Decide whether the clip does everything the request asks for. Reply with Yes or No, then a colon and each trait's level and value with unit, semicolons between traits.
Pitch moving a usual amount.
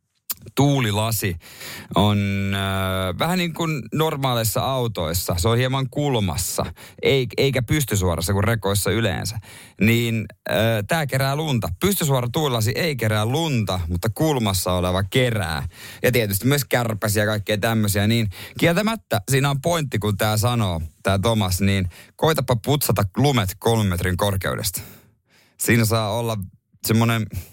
Yes: average, 4.7 semitones